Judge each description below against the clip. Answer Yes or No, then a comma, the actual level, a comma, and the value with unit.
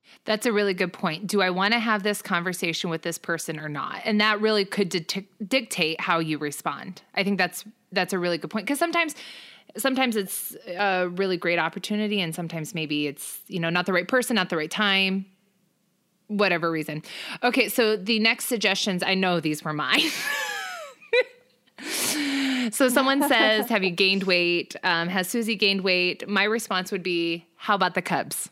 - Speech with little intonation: No, average, 4.1 semitones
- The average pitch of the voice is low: No, high, 195 Hz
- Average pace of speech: Yes, average, 185 wpm